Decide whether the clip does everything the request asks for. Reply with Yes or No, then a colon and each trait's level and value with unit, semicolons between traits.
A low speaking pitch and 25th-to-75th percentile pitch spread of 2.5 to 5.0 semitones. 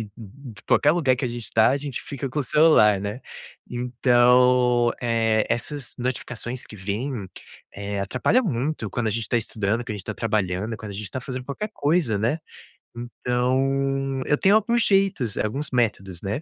Yes: low, 120 Hz; average, 4.0 semitones